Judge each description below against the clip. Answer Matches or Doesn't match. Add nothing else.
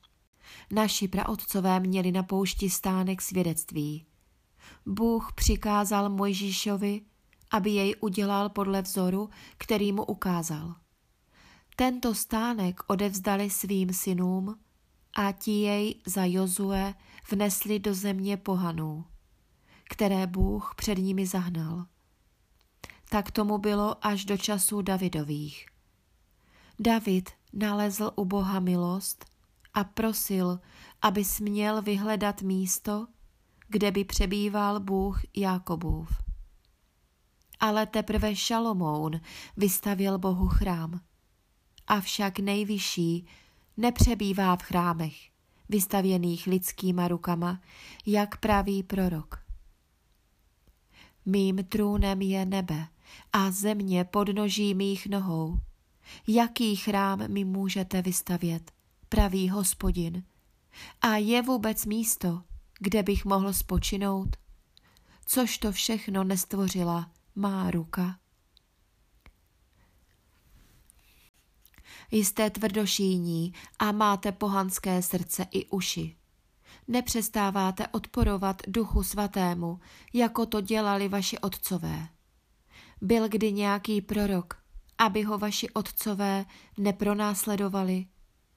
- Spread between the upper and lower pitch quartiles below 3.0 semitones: Matches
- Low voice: Doesn't match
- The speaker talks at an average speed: Doesn't match